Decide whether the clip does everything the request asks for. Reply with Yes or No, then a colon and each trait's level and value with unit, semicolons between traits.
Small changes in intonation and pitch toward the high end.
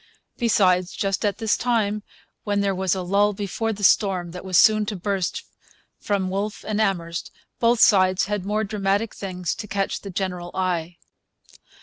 Yes: narrow, 2.2 semitones; high, 195 Hz